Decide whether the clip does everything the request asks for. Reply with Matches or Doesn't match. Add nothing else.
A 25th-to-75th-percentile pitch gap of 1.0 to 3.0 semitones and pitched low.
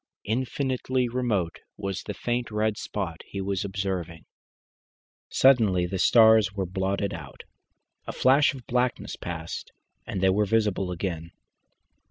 Doesn't match